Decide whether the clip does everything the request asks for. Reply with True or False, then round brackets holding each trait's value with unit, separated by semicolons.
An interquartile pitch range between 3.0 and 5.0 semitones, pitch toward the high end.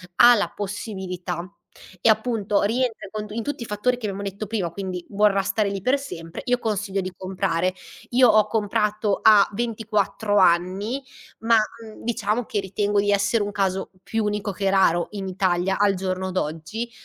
False (2.4 semitones; 205 Hz)